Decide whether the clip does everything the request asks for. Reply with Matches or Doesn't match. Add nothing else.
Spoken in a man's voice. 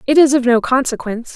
Doesn't match